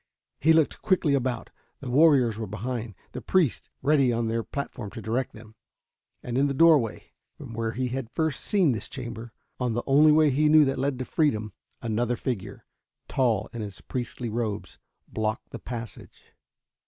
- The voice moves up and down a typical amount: Yes, average, 3.9 semitones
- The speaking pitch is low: Yes, low, 125 Hz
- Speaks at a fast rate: No, average, 175 wpm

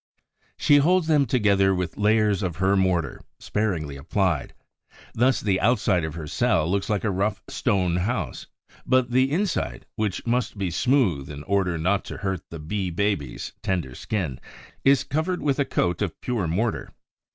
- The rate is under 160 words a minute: No, average, 165 wpm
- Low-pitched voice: Yes, low, 100 Hz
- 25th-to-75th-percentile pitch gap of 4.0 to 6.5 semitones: Yes, wide, 5.6 semitones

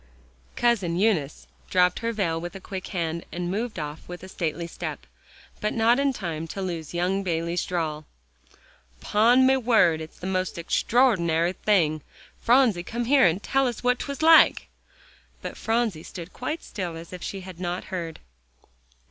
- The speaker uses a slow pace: No, average, 165 wpm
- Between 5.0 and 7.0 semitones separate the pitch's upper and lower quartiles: Yes, average, 5.3 semitones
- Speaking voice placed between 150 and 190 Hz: Yes, medium, 185 Hz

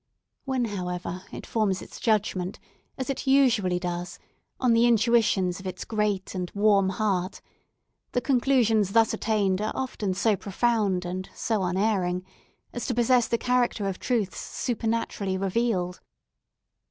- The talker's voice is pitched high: Yes, high, 210 Hz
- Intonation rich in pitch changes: No, average, 3.8 semitones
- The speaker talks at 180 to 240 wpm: No, average, 140 wpm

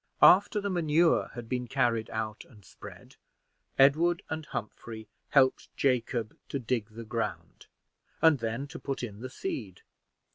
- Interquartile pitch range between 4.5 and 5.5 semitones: Yes, average, 4.8 semitones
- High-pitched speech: No, low, 125 Hz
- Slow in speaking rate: No, average, 145 wpm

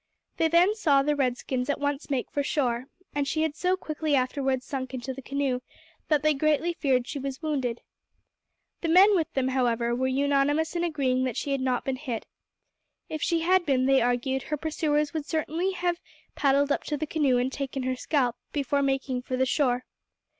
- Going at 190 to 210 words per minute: Yes, average, 200 wpm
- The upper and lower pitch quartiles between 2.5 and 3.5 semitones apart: Yes, average, 3.0 semitones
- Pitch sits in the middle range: No, very high, 280 Hz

